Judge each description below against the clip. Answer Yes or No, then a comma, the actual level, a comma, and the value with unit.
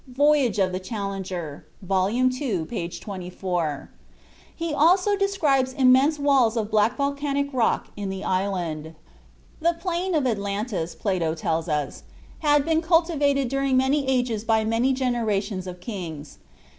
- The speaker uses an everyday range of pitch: No, wide, 7.0 semitones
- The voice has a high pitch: Yes, high, 235 Hz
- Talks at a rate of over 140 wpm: No, slow, 135 wpm